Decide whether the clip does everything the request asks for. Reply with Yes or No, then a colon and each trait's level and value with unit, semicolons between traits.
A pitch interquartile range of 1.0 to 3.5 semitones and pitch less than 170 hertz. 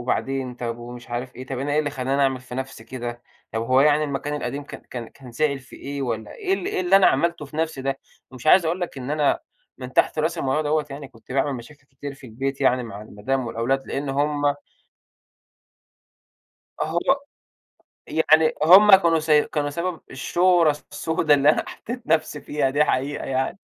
Yes: average, 3.1 semitones; medium, 140 Hz